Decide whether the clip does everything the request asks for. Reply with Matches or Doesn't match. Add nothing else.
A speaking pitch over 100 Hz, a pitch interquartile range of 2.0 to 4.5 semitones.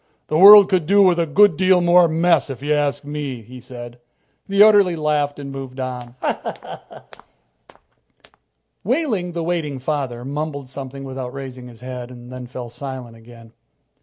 Doesn't match